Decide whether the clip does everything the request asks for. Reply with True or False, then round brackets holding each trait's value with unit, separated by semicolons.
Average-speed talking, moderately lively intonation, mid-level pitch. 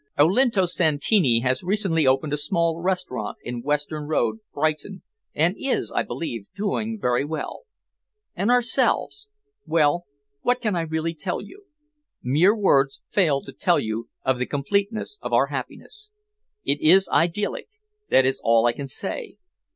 False (150 wpm; 6.2 semitones; 165 Hz)